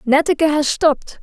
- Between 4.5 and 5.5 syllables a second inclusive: Yes, 5.4 syllables/s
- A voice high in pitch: Yes, very high, 300 Hz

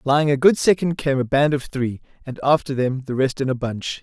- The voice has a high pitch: No, medium, 140 Hz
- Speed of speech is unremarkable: No, fast, 255 wpm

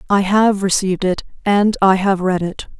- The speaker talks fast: No, average, 195 wpm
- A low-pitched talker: No, high, 195 Hz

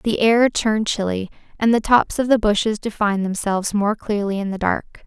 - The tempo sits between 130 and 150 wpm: No, average, 200 wpm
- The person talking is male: No, female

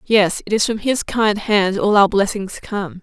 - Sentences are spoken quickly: Yes, fast, 220 wpm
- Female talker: Yes, female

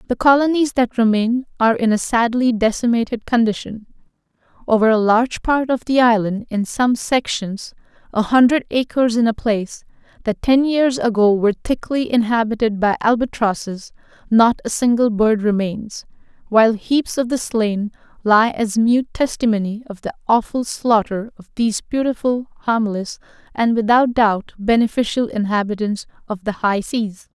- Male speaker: No, female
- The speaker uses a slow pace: No, average, 145 wpm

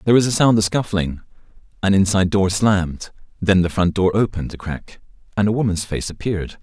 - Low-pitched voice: Yes, low, 100 Hz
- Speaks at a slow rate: No, average, 200 wpm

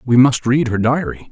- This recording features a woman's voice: No, male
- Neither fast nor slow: No, fast, 230 wpm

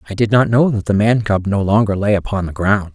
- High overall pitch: No, low, 105 Hz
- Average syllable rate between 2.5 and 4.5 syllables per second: No, 5.8 syllables/s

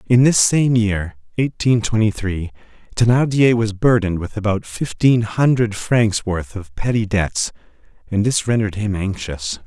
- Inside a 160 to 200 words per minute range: No, average, 150 wpm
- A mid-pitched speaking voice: No, low, 105 Hz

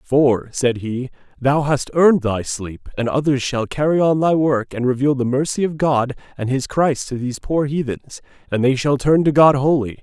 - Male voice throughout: Yes, male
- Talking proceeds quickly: Yes, fast, 210 wpm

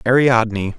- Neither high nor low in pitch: No, low, 115 Hz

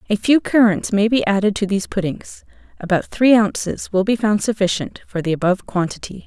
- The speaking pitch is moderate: No, high, 205 Hz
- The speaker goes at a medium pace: Yes, average, 190 wpm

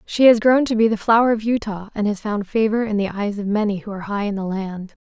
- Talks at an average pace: No, fast, 285 wpm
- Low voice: No, high, 210 Hz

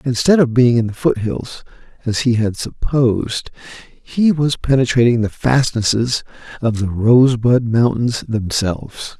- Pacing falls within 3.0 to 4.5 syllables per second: Yes, 4.4 syllables/s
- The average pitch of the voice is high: No, low, 120 Hz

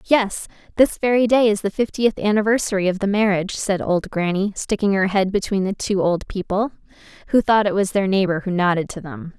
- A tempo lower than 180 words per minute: No, fast, 205 wpm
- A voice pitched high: Yes, high, 200 Hz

